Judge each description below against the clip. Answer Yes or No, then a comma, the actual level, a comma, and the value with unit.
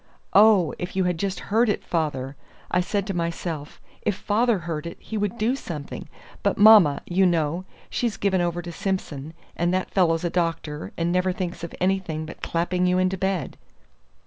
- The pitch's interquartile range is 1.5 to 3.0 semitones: Yes, average, 2.7 semitones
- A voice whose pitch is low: No, medium, 180 Hz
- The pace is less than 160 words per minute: No, average, 185 wpm